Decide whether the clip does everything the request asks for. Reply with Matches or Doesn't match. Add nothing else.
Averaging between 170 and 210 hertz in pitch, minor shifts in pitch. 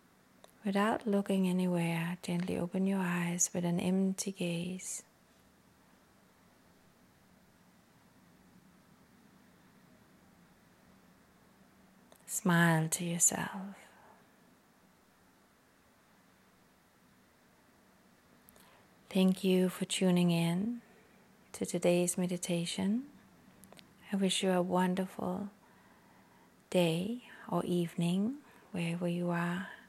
Matches